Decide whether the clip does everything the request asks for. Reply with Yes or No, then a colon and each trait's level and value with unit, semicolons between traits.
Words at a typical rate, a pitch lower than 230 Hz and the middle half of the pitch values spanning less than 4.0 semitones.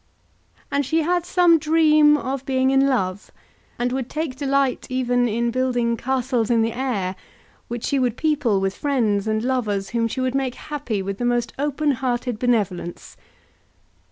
No: average, 165 wpm; very high, 255 Hz; average, 3.2 semitones